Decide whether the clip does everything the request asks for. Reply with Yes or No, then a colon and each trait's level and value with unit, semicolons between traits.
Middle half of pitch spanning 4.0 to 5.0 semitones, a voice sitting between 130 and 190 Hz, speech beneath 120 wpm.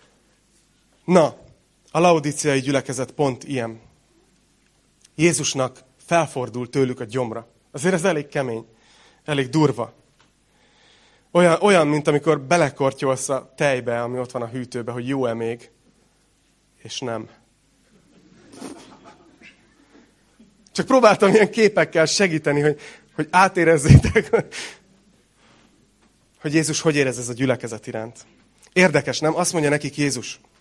Yes: average, 4.5 semitones; medium, 140 Hz; average, 110 wpm